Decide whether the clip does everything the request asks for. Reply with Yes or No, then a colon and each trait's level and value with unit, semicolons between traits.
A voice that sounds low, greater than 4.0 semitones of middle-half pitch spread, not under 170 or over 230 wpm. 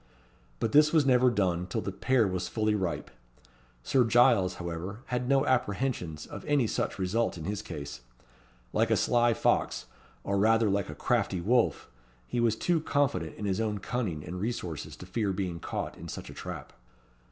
Yes: low, 105 Hz; average, 4.9 semitones; average, 180 wpm